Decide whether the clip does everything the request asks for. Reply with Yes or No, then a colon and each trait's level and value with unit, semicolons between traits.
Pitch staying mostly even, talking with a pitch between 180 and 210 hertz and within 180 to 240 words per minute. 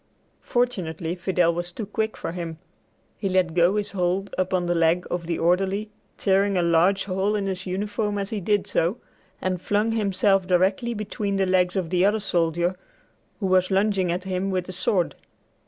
Yes: narrow, 2.3 semitones; medium, 185 Hz; average, 185 wpm